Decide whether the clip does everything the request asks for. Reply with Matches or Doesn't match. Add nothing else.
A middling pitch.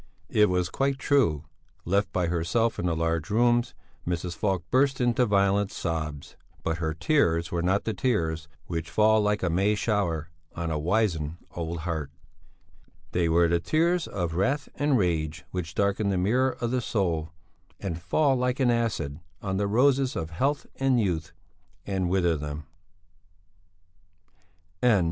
Doesn't match